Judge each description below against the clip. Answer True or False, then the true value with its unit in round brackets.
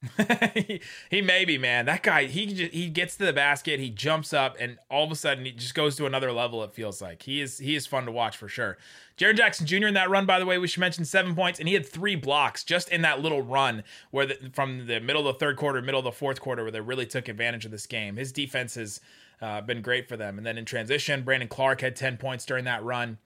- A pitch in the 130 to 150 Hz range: True (135 Hz)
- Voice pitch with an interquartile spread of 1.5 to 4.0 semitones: False (4.5 semitones)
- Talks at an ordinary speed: False (270 wpm)